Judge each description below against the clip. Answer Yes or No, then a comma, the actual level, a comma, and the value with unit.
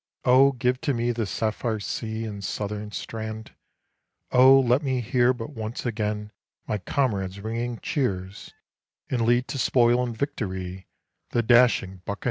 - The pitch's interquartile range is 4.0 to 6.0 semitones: No, average, 3.0 semitones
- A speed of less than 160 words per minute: Yes, average, 145 wpm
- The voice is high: No, low, 115 Hz